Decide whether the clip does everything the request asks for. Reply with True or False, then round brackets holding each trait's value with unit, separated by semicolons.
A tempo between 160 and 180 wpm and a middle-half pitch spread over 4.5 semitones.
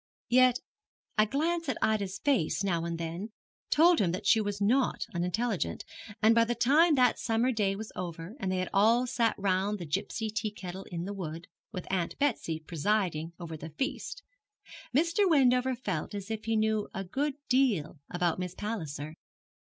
True (175 wpm; 5.5 semitones)